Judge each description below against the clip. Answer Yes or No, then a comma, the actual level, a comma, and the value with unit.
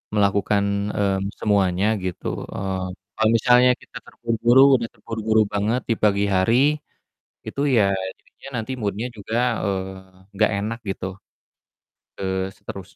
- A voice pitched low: Yes, low, 105 Hz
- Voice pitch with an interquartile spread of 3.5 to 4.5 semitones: No, average, 2.8 semitones